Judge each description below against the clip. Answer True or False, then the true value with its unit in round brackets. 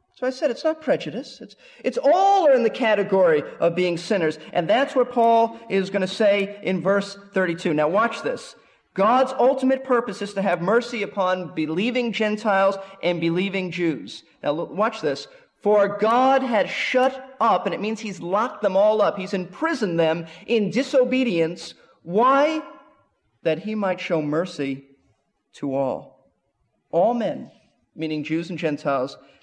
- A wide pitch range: True (6.1 semitones)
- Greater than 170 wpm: False (155 wpm)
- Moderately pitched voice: False (205 Hz)